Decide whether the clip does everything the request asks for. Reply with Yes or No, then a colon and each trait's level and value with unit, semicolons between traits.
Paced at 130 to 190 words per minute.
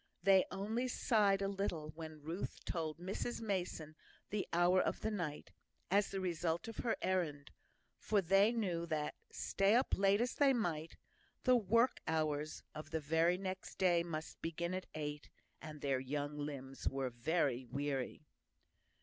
Yes: average, 160 wpm